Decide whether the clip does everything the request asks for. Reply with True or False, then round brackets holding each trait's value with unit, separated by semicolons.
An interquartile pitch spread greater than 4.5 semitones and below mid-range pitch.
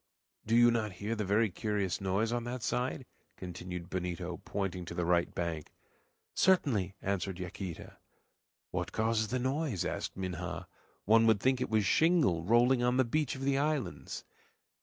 True (5.1 semitones; 110 Hz)